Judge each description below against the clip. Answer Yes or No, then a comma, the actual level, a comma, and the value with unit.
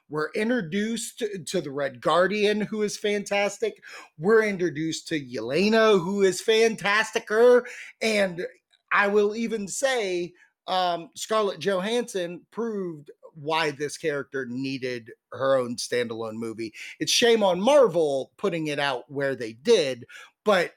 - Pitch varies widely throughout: Yes, wide, 6.3 semitones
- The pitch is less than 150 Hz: No, high, 195 Hz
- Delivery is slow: Yes, slow, 125 wpm